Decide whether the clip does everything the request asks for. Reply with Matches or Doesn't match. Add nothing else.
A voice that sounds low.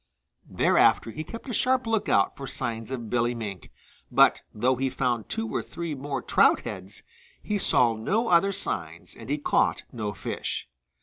Matches